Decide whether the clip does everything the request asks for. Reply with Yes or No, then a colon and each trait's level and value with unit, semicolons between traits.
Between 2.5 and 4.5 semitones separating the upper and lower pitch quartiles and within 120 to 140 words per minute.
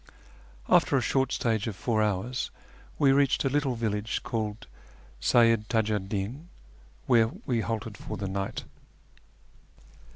Yes: average, 3.2 semitones; slow, 135 wpm